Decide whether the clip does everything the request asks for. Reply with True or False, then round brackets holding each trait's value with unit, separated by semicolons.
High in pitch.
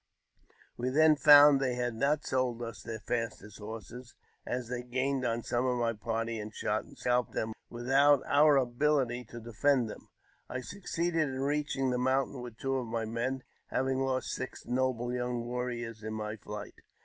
False (125 Hz)